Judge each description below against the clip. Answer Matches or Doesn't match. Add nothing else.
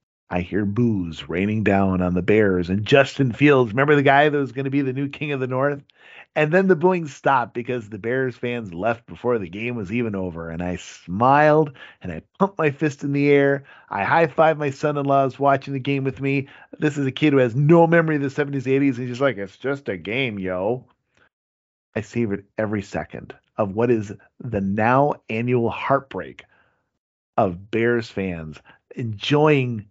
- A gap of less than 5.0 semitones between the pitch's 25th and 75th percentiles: Doesn't match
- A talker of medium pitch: Doesn't match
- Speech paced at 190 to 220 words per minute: Matches